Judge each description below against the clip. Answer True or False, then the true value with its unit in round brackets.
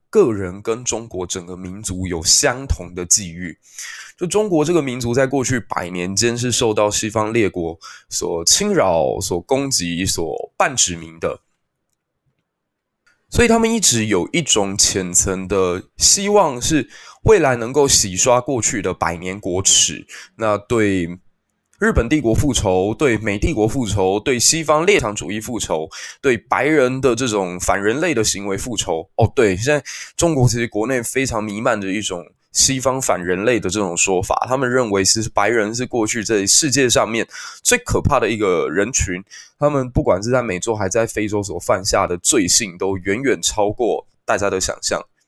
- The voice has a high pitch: False (110 Hz)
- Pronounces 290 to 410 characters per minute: False (255 characters per minute)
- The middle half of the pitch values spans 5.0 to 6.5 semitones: True (5.4 semitones)